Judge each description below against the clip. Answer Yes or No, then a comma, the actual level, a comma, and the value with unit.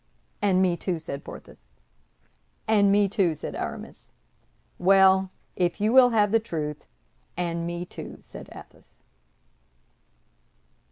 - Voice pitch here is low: No, high, 190 Hz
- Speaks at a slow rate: Yes, slow, 120 wpm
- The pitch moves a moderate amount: Yes, average, 3.1 semitones